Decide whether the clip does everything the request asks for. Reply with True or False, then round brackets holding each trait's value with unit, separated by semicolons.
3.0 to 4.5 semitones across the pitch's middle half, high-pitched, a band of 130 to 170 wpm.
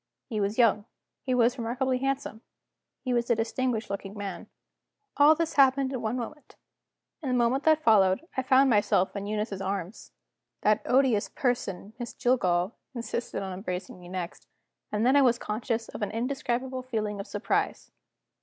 True (4.1 semitones; 235 Hz; 165 wpm)